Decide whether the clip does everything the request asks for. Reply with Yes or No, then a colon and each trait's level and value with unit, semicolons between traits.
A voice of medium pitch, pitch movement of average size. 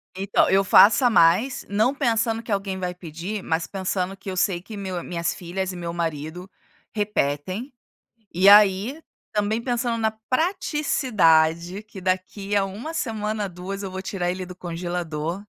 No: high, 195 Hz; average, 3.4 semitones